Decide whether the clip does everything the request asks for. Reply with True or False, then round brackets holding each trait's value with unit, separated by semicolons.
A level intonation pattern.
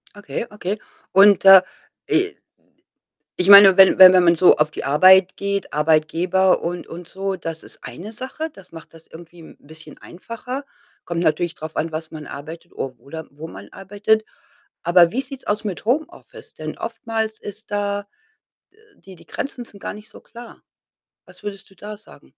False (4.1 semitones)